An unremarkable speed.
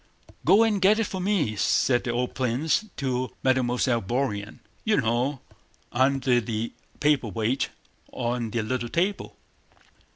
No: slow, 125 wpm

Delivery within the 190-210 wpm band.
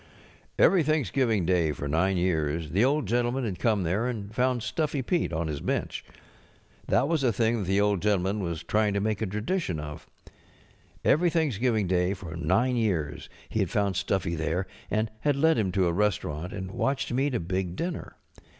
Yes: average, 195 wpm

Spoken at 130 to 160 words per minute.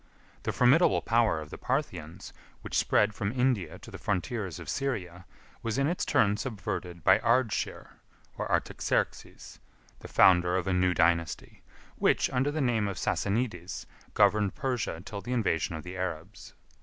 Yes: average, 155 wpm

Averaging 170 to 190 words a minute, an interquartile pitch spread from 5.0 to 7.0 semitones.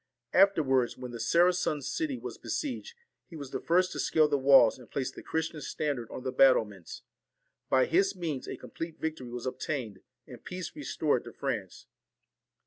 Yes: average, 175 wpm; average, 5.3 semitones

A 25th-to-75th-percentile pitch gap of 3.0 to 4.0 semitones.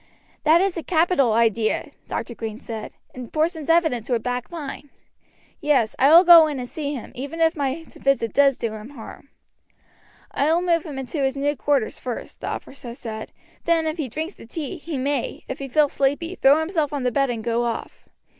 No: average, 4.6 semitones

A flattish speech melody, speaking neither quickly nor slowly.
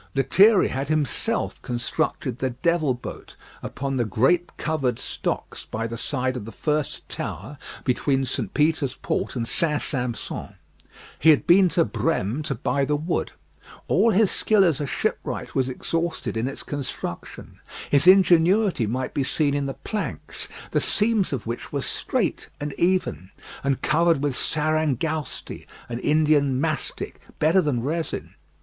No: average, 4.2 semitones; average, 150 wpm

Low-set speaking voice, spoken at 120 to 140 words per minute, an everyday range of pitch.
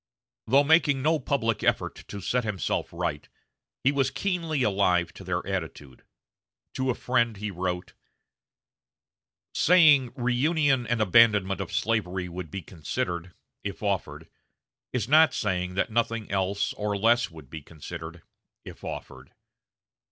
No: low, 105 Hz; slow, 135 wpm; wide, 5.9 semitones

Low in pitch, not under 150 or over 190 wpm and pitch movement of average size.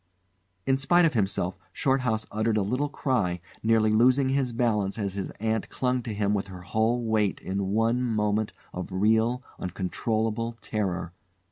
Yes: low, 110 Hz; average, 155 wpm; average, 3.4 semitones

